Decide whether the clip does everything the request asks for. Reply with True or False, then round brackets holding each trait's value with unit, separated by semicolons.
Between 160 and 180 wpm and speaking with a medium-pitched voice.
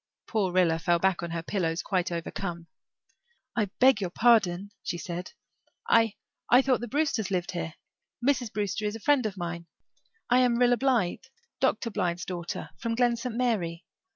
False (170 wpm; 205 Hz)